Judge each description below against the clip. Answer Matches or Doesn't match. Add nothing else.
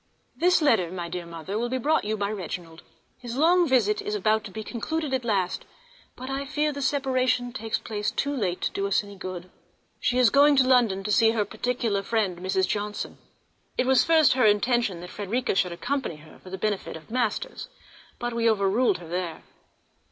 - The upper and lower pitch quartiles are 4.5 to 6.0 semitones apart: Matches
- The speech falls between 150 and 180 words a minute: Doesn't match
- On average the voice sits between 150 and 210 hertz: Doesn't match